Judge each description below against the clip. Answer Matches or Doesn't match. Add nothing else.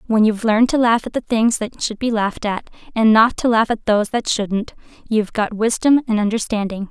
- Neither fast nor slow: Doesn't match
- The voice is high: Matches